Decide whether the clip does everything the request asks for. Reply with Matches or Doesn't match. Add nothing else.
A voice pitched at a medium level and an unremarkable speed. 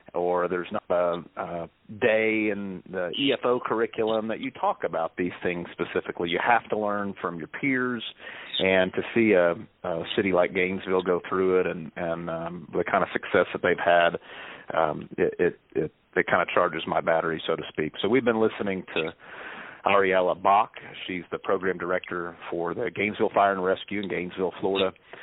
Doesn't match